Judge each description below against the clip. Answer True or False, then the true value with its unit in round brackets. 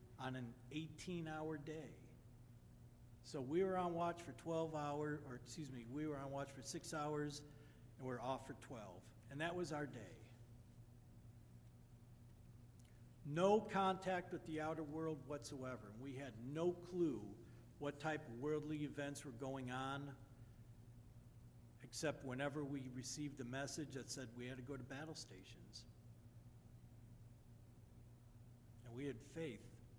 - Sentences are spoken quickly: False (145 wpm)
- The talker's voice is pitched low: True (130 Hz)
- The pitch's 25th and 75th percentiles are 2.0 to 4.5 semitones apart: True (4.1 semitones)